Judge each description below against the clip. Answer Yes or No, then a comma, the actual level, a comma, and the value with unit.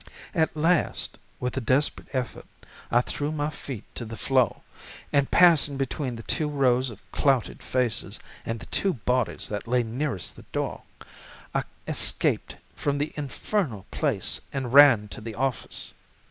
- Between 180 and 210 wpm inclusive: No, average, 155 wpm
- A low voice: Yes, low, 130 Hz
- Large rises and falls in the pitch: No, average, 3.6 semitones